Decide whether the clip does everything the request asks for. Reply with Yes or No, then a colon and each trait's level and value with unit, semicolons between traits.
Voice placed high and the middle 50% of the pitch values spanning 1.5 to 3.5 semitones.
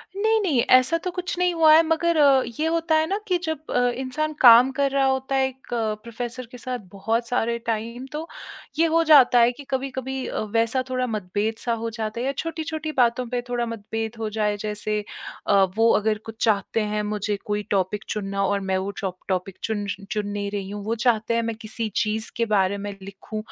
No: high, 235 Hz; average, 4.0 semitones